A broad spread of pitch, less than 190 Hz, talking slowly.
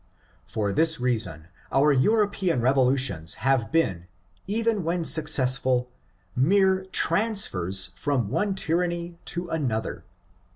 Yes: wide, 6.8 semitones; medium, 140 Hz; slow, 110 wpm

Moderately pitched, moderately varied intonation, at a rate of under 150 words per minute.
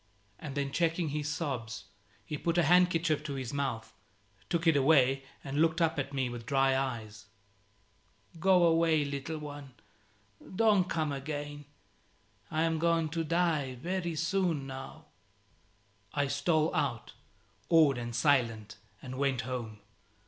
Yes: medium, 145 Hz; average, 3.5 semitones; average, 140 wpm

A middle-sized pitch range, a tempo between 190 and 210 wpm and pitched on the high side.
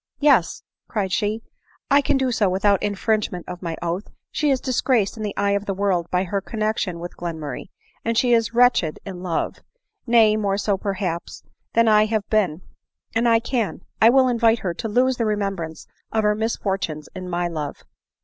Yes: average, 3.9 semitones; average, 195 wpm; high, 205 Hz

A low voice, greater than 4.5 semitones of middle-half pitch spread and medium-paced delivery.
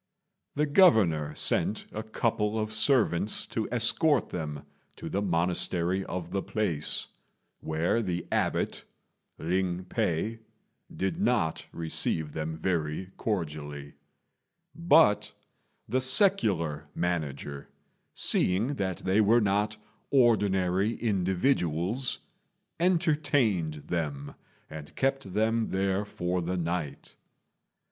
No: very low, 95 Hz; average, 5.3 semitones; slow, 100 wpm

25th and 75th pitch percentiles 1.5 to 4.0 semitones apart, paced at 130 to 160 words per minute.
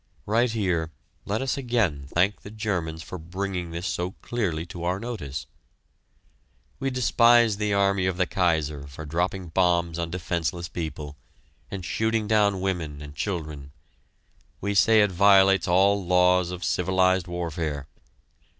Yes: average, 3.4 semitones; average, 140 wpm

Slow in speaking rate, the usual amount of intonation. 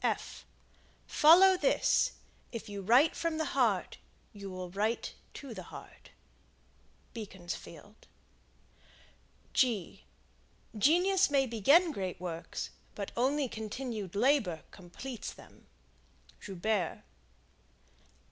No: slow, 90 wpm; wide, 6.5 semitones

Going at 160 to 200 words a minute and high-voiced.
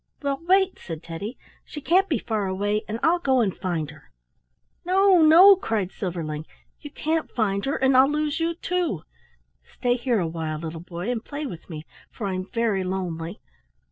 Yes: average, 175 wpm; high, 220 Hz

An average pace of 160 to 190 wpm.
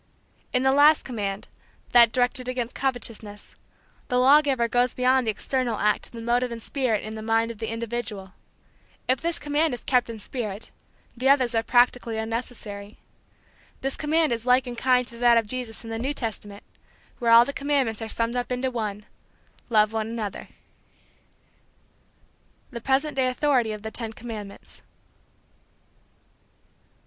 Yes: average, 165 wpm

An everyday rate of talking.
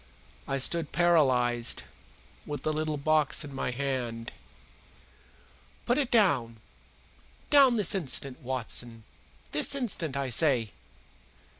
No: slow, 110 wpm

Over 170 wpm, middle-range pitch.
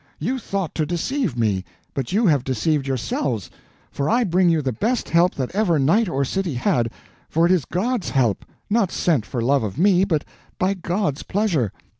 Yes: average, 190 wpm; medium, 165 Hz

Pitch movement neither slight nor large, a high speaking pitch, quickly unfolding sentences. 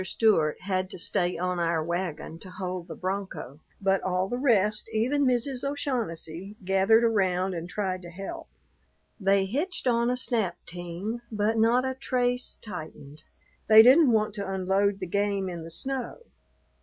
No: average, 4.5 semitones; high, 195 Hz; average, 160 wpm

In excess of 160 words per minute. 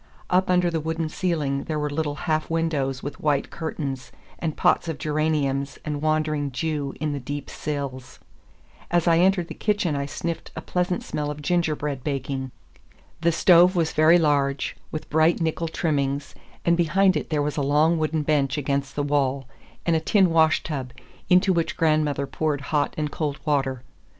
Yes: average, 175 wpm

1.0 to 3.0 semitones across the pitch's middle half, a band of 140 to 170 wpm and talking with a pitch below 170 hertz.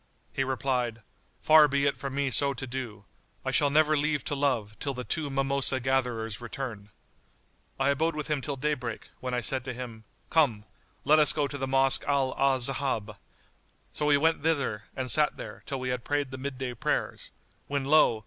No: narrow, 2.4 semitones; average, 190 wpm; low, 135 Hz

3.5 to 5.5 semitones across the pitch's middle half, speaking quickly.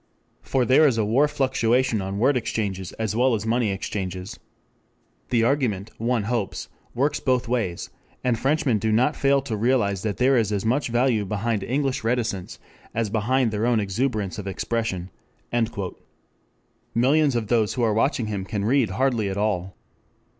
No: average, 3.8 semitones; average, 170 wpm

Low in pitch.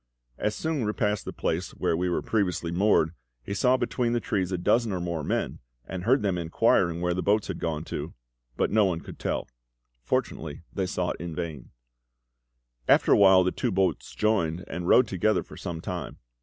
Yes: very low, 90 Hz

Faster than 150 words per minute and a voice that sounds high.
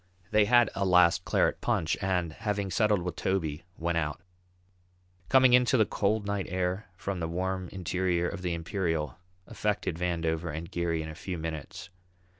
No: average, 170 wpm; very low, 90 Hz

